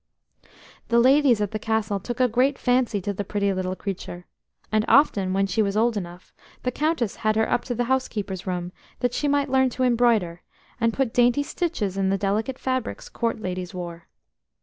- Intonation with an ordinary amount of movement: Yes, average, 4.4 semitones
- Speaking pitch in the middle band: No, high, 220 Hz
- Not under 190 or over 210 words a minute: Yes, average, 195 wpm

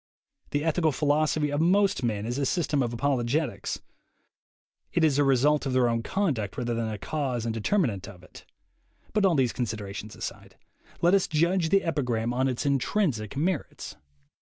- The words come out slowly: No, average, 170 wpm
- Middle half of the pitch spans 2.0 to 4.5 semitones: No, wide, 5.4 semitones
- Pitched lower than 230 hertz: Yes, medium, 140 Hz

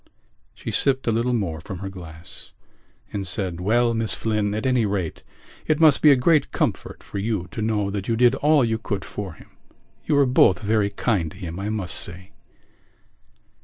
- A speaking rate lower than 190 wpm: No, average, 195 wpm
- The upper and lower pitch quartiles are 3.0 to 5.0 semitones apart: Yes, average, 4.0 semitones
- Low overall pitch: Yes, low, 105 Hz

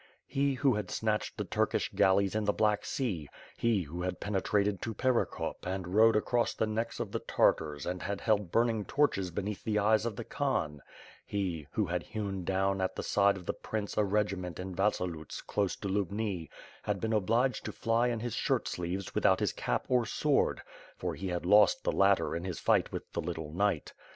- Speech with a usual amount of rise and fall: Yes, average, 3.3 semitones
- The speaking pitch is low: Yes, low, 100 Hz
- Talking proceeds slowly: No, fast, 205 wpm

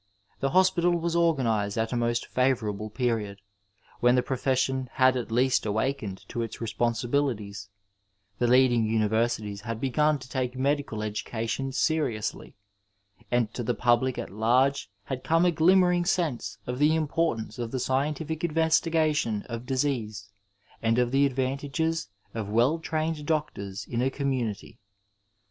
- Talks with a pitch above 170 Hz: No, low, 125 Hz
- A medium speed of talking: Yes, average, 145 wpm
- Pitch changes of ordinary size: Yes, average, 4.5 semitones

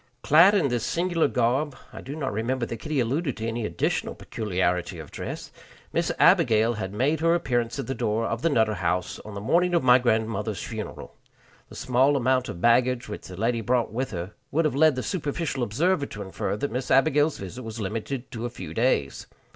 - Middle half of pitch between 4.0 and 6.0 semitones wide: Yes, average, 4.4 semitones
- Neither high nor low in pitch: No, low, 120 Hz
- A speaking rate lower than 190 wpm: No, fast, 205 wpm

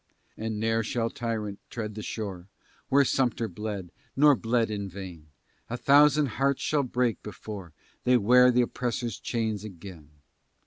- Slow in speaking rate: No, average, 145 wpm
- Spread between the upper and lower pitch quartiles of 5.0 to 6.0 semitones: No, average, 3.5 semitones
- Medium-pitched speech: No, low, 115 Hz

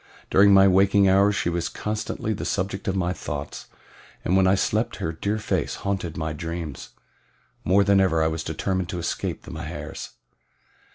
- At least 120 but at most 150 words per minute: No, average, 175 wpm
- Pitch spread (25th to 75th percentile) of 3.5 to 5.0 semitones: No, average, 3.1 semitones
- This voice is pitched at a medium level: No, very low, 95 Hz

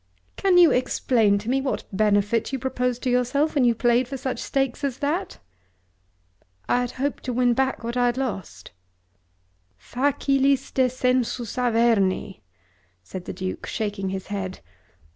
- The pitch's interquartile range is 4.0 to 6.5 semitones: No, average, 3.6 semitones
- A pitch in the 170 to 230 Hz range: No, high, 245 Hz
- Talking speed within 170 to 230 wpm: No, average, 145 wpm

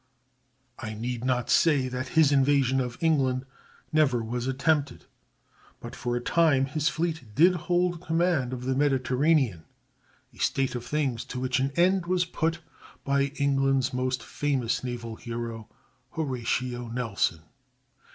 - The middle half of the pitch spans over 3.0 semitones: Yes, average, 3.9 semitones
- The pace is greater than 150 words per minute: No, average, 140 wpm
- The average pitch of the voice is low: Yes, low, 130 Hz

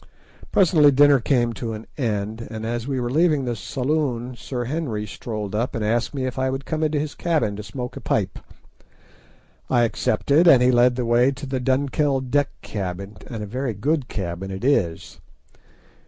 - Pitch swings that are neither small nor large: Yes, average, 4.0 semitones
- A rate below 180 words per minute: No, average, 185 wpm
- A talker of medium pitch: No, low, 125 Hz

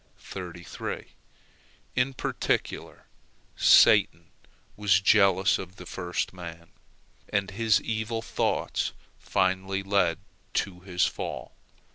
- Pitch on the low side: Yes, very low, 95 Hz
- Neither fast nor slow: No, slow, 90 wpm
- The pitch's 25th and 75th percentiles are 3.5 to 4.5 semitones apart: No, narrow, 2.4 semitones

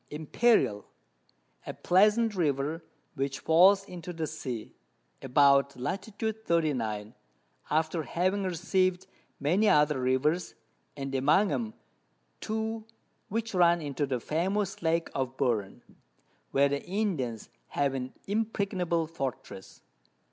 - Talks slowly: Yes, slow, 110 wpm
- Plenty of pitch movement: Yes, wide, 5.9 semitones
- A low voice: No, medium, 160 Hz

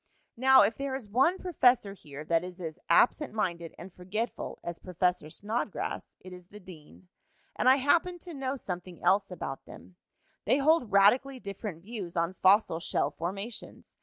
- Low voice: No, high, 200 Hz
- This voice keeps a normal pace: Yes, average, 165 wpm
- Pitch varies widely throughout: Yes, wide, 6.5 semitones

